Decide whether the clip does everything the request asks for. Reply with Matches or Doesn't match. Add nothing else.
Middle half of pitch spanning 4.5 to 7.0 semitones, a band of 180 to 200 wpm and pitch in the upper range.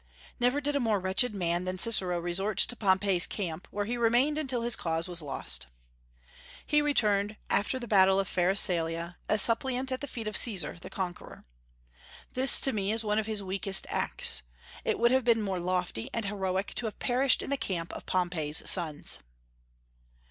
Matches